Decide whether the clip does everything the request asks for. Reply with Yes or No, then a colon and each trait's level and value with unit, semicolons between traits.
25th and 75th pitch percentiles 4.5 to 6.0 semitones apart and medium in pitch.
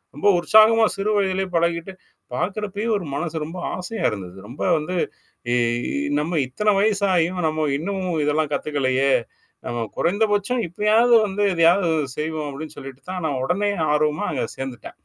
Yes: average, 5.2 semitones; medium, 170 Hz